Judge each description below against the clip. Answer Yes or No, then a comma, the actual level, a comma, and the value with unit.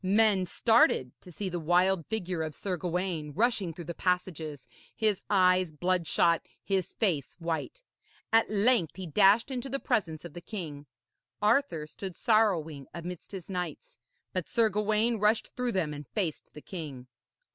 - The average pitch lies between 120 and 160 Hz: No, medium, 185 Hz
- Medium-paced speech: Yes, average, 155 wpm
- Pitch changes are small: No, average, 4.6 semitones